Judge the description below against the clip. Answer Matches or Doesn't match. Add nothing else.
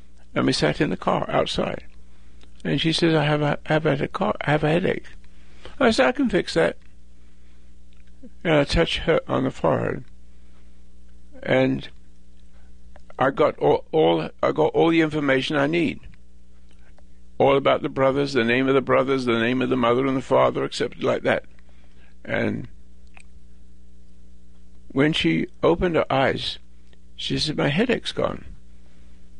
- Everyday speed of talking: Matches